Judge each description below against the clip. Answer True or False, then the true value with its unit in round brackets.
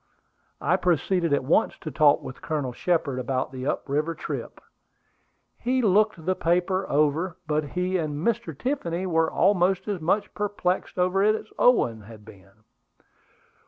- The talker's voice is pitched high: False (170 Hz)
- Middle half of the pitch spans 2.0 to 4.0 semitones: False (4.8 semitones)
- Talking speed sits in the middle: True (155 wpm)